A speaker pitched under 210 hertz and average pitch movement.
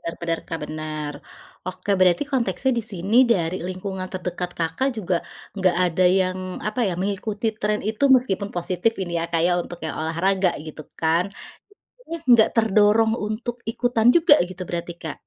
Yes: medium, 185 Hz; average, 4.1 semitones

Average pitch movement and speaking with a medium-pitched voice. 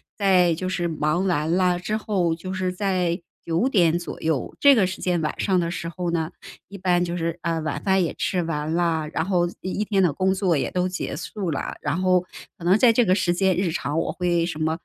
No: narrow, 2.2 semitones; medium, 175 Hz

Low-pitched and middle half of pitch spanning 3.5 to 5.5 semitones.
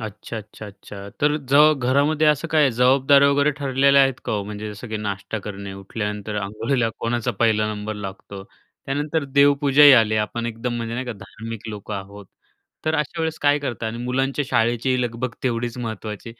Yes: low, 120 Hz; average, 4.6 semitones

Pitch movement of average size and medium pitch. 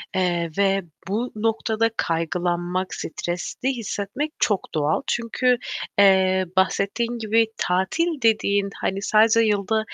No: average, 3.4 semitones; high, 200 Hz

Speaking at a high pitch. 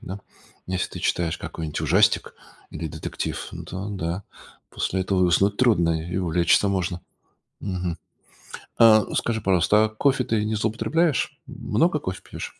No: very low, 95 Hz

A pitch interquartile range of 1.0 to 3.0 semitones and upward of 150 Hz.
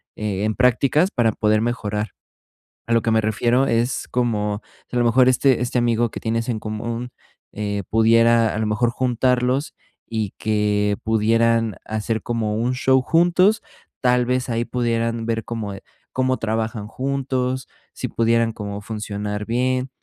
No: narrow, 2.5 semitones; low, 115 Hz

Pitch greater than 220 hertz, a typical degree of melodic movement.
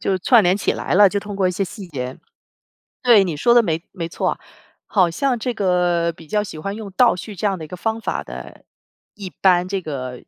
No: high, 190 Hz; average, 3.6 semitones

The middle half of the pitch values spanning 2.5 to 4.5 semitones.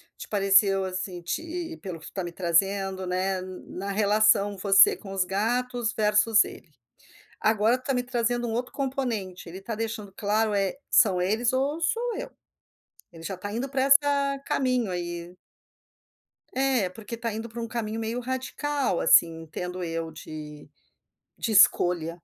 No: average, 4.9 semitones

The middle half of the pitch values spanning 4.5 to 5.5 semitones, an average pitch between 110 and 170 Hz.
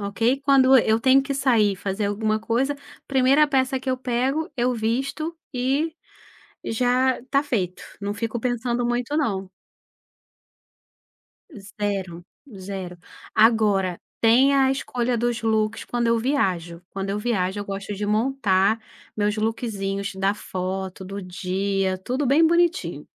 No: average, 4.8 semitones; high, 225 Hz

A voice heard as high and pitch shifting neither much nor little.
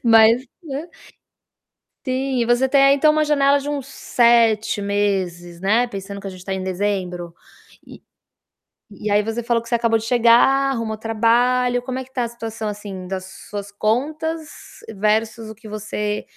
Yes: high, 225 Hz; average, 3.7 semitones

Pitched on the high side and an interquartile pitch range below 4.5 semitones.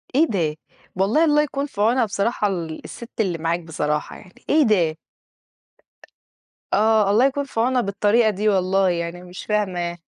No: high, 200 Hz; average, 4.9 semitones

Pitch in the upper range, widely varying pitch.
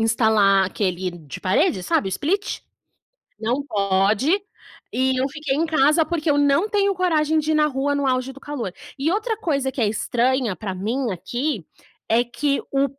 Yes: very high, 270 Hz; wide, 5.8 semitones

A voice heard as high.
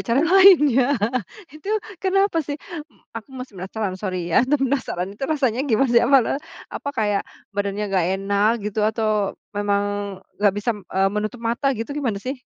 Yes: high, 220 Hz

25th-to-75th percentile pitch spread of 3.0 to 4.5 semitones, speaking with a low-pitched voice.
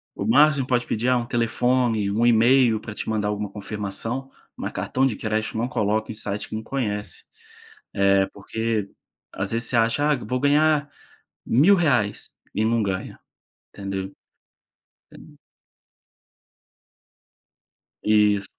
Yes: average, 3.4 semitones; low, 110 Hz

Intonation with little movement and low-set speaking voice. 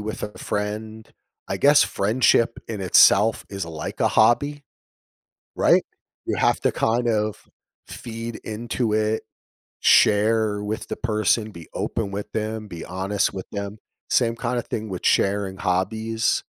Yes: narrow, 2.0 semitones; low, 110 Hz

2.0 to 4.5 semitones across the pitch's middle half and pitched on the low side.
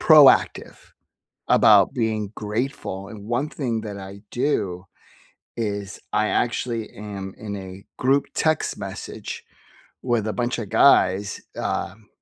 Yes: average, 3.4 semitones; low, 110 Hz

